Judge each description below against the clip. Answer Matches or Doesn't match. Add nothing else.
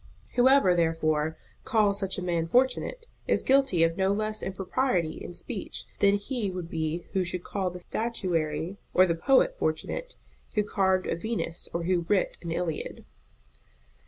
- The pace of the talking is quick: Doesn't match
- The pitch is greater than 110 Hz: Matches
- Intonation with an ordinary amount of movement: Matches